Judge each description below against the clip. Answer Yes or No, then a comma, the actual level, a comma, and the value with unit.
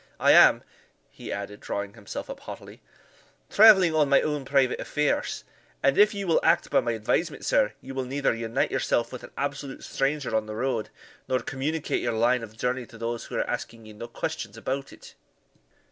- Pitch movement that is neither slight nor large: Yes, average, 4.1 semitones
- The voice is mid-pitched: No, low, 130 Hz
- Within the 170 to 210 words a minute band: Yes, average, 190 wpm